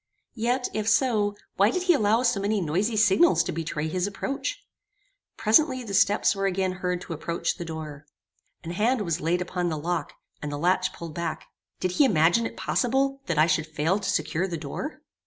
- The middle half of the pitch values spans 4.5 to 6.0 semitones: Yes, average, 4.9 semitones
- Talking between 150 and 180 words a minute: No, average, 195 wpm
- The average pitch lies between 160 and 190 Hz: Yes, medium, 185 Hz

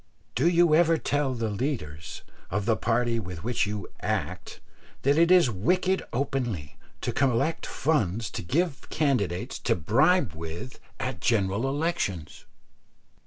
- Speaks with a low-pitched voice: Yes, low, 120 Hz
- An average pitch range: No, wide, 7.6 semitones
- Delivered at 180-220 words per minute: No, slow, 135 wpm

